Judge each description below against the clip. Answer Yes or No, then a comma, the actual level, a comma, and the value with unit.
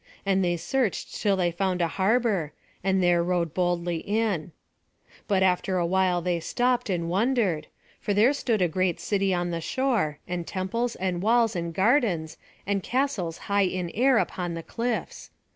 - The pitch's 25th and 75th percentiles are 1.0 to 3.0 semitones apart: No, average, 4.2 semitones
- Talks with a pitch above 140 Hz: Yes, high, 190 Hz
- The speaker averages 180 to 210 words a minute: No, average, 165 wpm